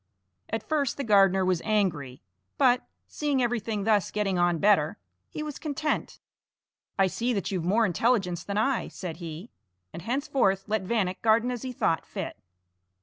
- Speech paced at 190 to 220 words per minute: No, average, 160 wpm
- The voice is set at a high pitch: Yes, high, 210 Hz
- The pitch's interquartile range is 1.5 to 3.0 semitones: No, average, 4.9 semitones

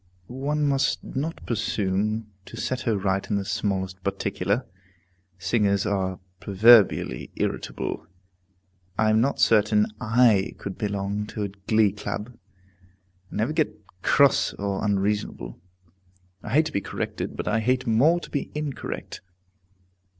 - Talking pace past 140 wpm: No, slow, 135 wpm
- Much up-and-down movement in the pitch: No, average, 3.7 semitones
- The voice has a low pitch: Yes, low, 105 Hz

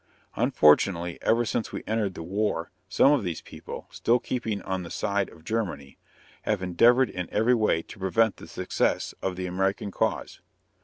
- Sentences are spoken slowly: No, average, 170 wpm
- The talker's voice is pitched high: No, low, 100 Hz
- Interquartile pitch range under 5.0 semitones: Yes, average, 4.0 semitones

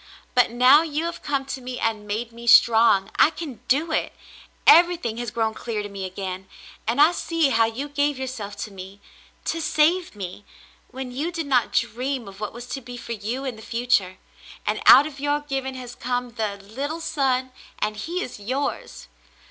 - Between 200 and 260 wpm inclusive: Yes, fast, 205 wpm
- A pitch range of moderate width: Yes, average, 4.6 semitones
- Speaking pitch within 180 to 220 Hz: No, very high, 250 Hz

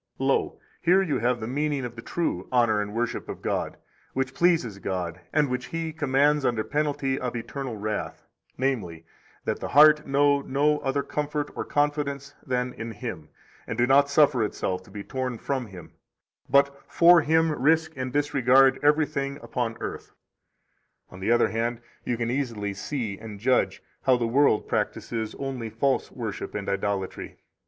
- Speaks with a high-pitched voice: No, low, 130 Hz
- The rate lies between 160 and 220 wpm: Yes, average, 170 wpm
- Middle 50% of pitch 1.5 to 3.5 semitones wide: No, average, 4.2 semitones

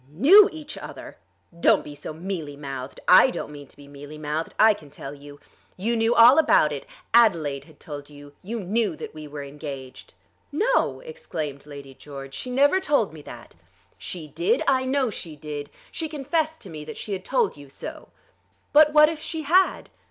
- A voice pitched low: No, medium, 170 Hz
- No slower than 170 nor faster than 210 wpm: Yes, average, 190 wpm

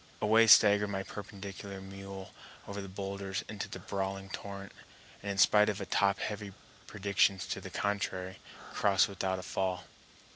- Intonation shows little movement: Yes, narrow, 1.0 semitones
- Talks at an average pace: Yes, average, 150 wpm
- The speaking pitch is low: Yes, low, 100 Hz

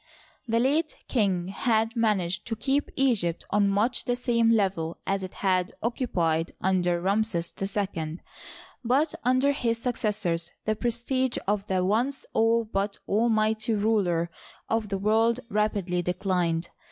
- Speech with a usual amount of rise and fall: Yes, average, 4.1 semitones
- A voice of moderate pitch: No, high, 215 Hz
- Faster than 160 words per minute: No, average, 140 wpm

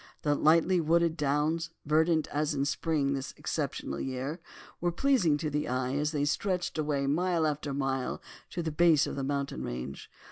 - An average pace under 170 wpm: No, average, 180 wpm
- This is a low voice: No, medium, 150 Hz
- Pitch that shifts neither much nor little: Yes, average, 3.0 semitones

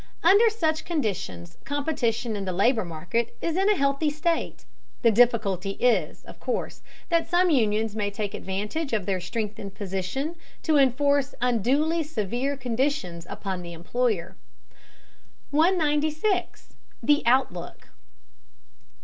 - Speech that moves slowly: Yes, slow, 125 wpm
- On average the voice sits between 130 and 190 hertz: No, high, 245 Hz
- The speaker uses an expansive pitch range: Yes, wide, 7.1 semitones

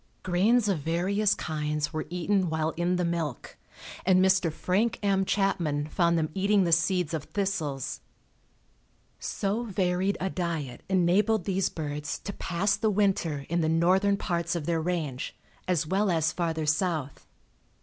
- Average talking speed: Yes, average, 150 wpm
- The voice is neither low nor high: Yes, medium, 175 Hz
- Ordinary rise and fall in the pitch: Yes, average, 3.4 semitones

